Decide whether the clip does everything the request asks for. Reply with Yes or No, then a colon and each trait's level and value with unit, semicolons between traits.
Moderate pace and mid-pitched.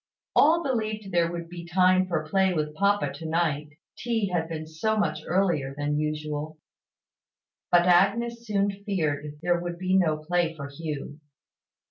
Yes: average, 155 wpm; medium, 175 Hz